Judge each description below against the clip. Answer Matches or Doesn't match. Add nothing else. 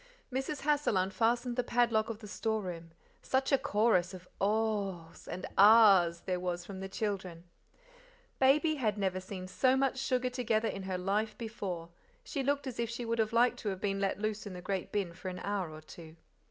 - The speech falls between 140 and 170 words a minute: Doesn't match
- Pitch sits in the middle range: Doesn't match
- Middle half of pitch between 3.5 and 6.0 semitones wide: Matches